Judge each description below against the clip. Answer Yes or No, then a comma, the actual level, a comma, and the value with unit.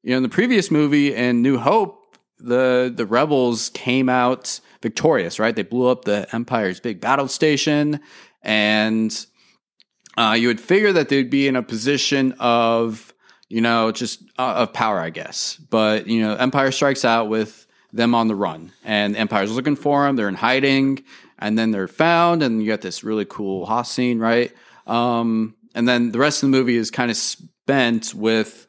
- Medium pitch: No, low, 120 Hz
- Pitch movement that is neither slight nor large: Yes, average, 3.5 semitones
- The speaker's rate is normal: Yes, average, 185 wpm